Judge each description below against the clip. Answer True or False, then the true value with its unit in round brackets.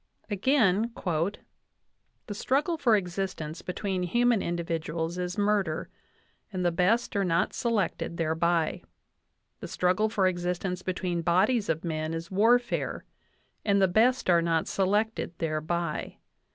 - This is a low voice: False (180 Hz)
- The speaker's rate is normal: False (125 wpm)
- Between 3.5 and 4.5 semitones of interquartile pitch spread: True (3.8 semitones)